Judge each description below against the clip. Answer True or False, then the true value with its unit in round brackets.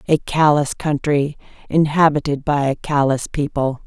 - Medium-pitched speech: True (145 Hz)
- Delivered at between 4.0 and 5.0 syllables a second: True (4.5 syllables/s)